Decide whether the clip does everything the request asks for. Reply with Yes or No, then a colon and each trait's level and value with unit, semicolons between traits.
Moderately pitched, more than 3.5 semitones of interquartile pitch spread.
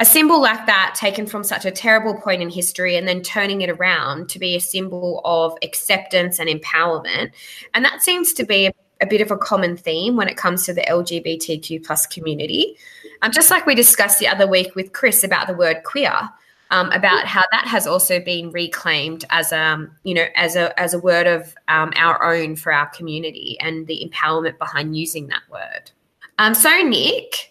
Yes: medium, 180 Hz; average, 4.1 semitones